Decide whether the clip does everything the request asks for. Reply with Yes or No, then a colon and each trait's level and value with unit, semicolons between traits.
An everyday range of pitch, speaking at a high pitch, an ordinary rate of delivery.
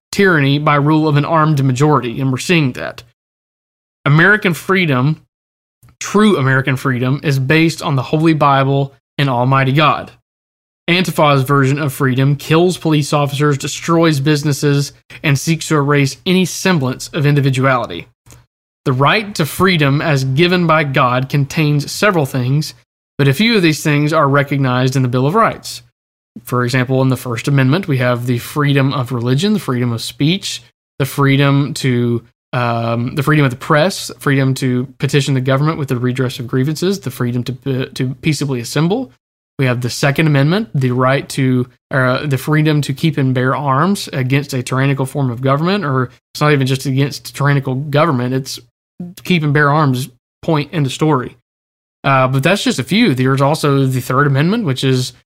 No: average, 3.0 semitones; medium, 140 Hz; average, 175 wpm